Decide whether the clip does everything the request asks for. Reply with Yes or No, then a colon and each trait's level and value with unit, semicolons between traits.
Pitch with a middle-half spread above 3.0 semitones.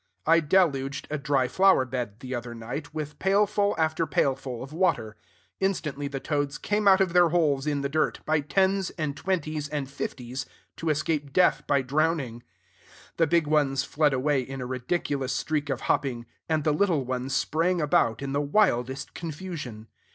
Yes: average, 3.6 semitones